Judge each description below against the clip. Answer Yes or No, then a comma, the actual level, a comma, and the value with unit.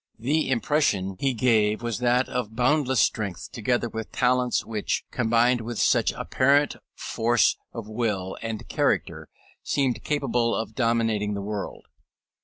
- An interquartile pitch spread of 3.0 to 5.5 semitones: No, narrow, 2.5 semitones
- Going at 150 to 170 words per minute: No, slow, 135 wpm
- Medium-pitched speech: No, low, 115 Hz